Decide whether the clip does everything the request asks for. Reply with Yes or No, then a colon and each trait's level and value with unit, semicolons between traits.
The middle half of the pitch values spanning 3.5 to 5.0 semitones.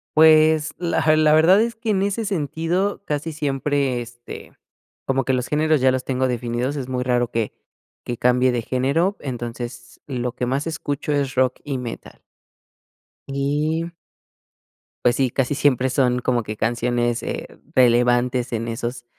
Yes: average, 4.0 semitones